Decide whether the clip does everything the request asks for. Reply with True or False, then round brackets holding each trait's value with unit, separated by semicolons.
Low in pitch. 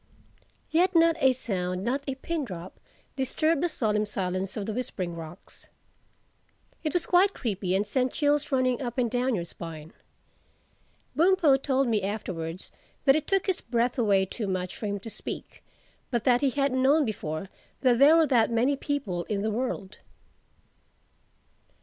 False (240 Hz)